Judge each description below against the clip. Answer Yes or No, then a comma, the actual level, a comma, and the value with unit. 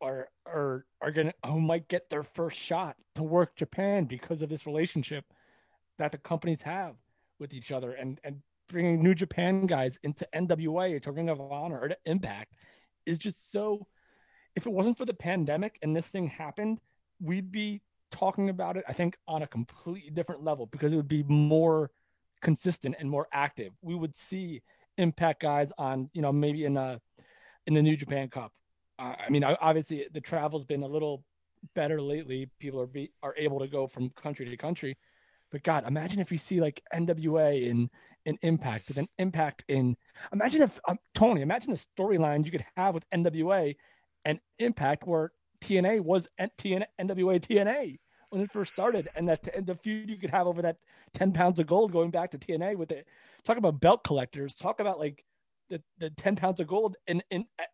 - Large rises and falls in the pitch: No, average, 4.2 semitones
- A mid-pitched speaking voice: Yes, medium, 160 Hz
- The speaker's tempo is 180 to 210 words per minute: Yes, average, 190 wpm